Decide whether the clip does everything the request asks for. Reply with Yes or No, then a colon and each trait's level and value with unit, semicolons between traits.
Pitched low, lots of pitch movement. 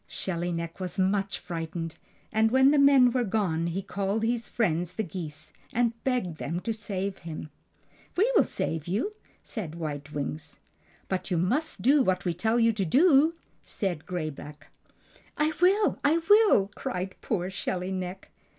No: high, 190 Hz; wide, 6.0 semitones